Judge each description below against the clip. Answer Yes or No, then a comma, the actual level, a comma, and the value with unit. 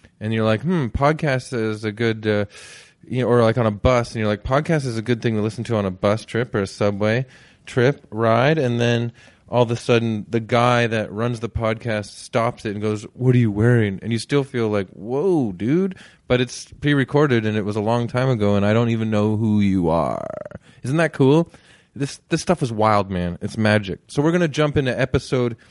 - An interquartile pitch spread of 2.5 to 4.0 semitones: Yes, average, 3.0 semitones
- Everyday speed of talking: No, fast, 230 wpm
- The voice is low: Yes, low, 115 Hz